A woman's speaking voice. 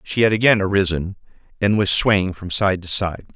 No: male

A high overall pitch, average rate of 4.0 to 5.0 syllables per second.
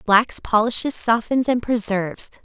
Yes: high, 225 Hz; 4.5 syllables/s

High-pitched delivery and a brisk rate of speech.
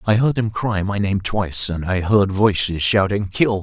No: low, 100 Hz; fast, 215 wpm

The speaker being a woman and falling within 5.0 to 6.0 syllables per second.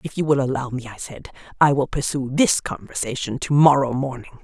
Yes: female; 5.5 syllables/s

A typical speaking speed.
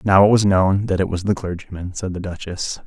No: fast, 250 wpm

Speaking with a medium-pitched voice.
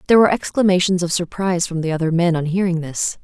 Yes: medium, 175 Hz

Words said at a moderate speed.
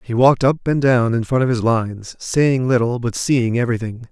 No: fast, 220 wpm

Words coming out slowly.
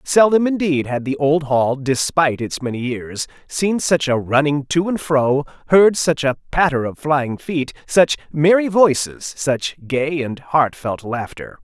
No: average, 170 wpm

